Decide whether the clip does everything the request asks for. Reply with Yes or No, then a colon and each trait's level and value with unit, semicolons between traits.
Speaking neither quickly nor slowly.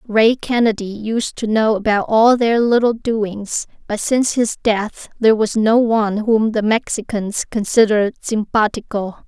Yes: average, 150 wpm